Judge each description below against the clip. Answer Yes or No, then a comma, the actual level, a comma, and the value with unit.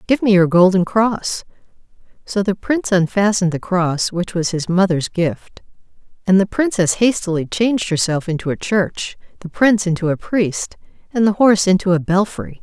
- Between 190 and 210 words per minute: No, average, 170 wpm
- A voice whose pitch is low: No, high, 190 Hz